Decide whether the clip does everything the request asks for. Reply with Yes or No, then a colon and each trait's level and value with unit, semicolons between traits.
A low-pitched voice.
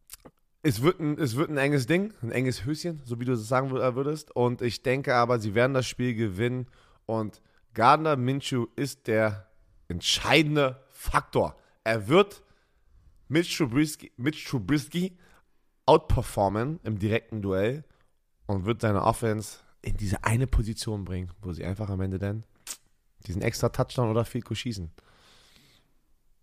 Yes: low, 120 Hz